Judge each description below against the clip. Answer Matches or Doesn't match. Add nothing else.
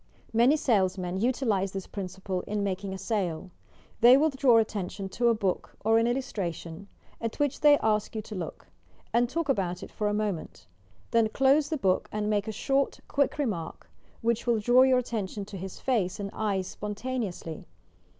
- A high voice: Matches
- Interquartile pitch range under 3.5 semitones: Doesn't match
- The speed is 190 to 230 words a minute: Doesn't match